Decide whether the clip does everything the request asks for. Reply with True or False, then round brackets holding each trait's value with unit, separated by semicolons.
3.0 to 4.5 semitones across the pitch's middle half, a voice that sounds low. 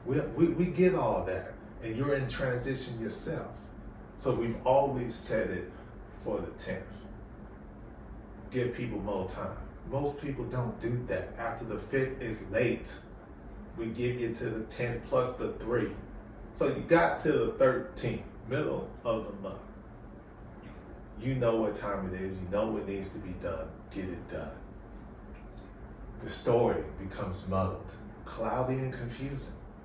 True (3.6 semitones; 115 Hz)